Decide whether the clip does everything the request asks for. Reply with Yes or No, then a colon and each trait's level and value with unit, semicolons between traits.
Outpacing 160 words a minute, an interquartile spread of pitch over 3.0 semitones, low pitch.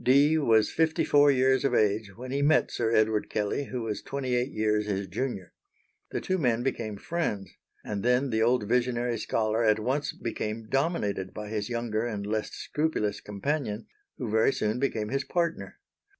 Yes: average, 180 wpm; average, 4.0 semitones; low, 115 Hz